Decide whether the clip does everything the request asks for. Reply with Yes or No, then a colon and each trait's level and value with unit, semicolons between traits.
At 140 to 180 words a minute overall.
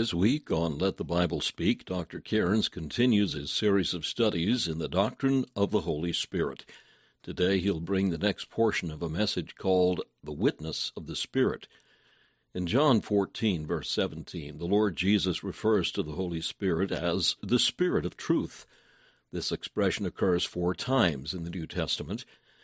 Yes: average, 165 wpm